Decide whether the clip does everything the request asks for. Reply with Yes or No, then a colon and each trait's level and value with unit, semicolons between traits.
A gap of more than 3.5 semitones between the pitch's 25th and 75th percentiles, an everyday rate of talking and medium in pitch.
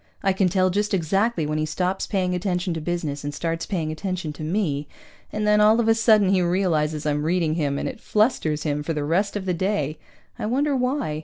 No: average, 4.9 semitones; fast, 225 wpm; medium, 180 Hz